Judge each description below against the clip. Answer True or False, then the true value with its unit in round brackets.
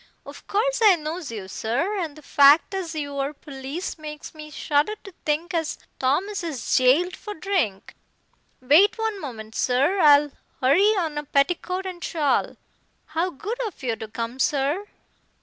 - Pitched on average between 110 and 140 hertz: False (305 Hz)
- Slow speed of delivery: False (165 wpm)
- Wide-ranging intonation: False (5.0 semitones)